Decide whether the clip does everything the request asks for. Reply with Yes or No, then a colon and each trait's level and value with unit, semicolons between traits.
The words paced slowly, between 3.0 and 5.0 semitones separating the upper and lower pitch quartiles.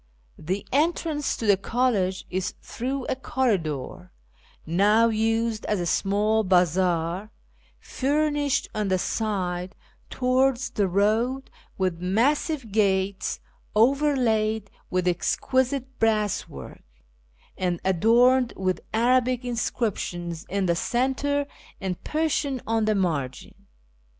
No: slow, 105 wpm; wide, 5.4 semitones